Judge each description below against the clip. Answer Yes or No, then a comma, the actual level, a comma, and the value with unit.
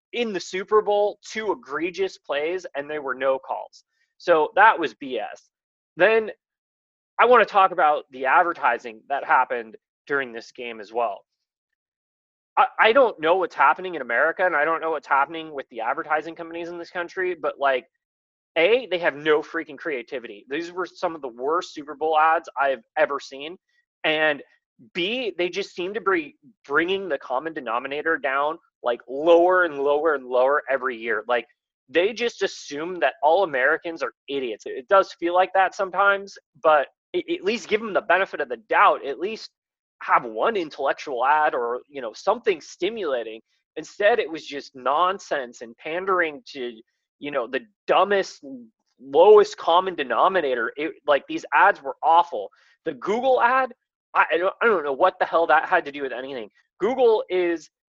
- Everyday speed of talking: Yes, average, 175 wpm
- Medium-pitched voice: Yes, medium, 180 Hz